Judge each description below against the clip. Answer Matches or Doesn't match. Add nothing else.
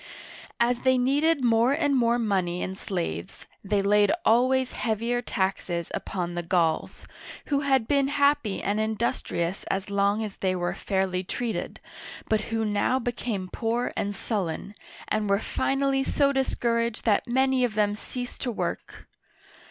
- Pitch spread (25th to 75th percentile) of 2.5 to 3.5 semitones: Doesn't match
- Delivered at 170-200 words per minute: Doesn't match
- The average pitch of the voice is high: Matches